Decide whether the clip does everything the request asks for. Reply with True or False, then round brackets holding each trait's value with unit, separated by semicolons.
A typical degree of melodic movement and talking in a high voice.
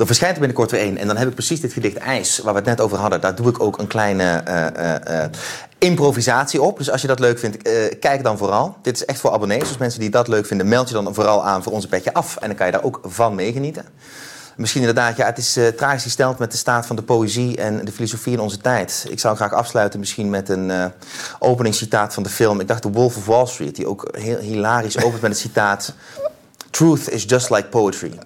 False (3.1 semitones; 115 Hz)